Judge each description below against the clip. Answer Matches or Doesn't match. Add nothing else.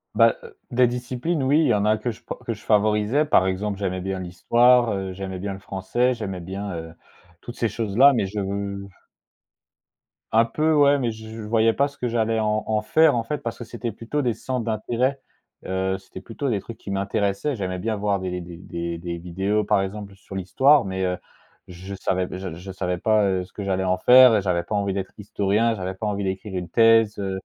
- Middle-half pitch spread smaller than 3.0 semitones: Doesn't match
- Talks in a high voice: Doesn't match